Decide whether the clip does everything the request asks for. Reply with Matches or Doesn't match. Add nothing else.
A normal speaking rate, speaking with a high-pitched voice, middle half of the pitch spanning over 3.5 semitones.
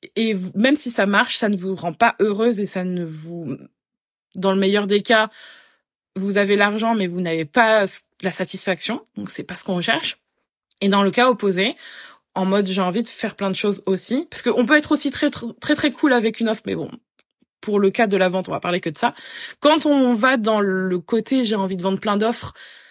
Doesn't match